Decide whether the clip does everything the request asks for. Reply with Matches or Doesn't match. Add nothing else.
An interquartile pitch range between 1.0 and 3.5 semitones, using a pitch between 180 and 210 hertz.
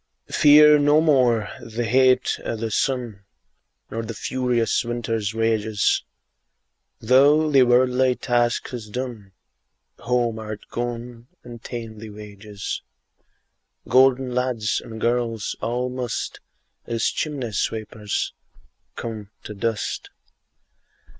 Doesn't match